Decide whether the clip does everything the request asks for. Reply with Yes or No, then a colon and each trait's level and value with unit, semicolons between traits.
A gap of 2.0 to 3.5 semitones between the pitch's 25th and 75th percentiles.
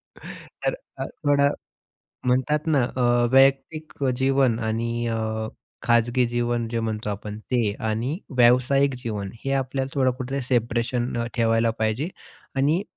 Yes: average, 2.8 semitones